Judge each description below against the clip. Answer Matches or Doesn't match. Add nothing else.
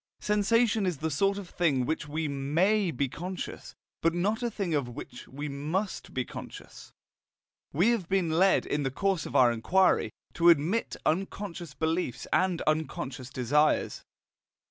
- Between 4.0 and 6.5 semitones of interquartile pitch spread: Matches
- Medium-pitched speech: Matches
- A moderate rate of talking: Matches